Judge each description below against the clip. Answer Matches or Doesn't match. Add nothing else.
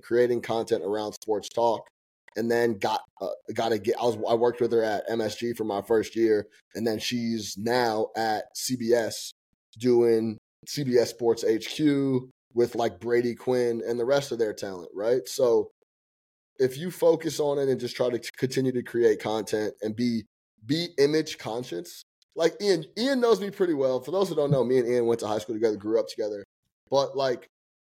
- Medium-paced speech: Matches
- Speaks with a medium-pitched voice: Doesn't match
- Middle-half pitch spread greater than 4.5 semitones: Matches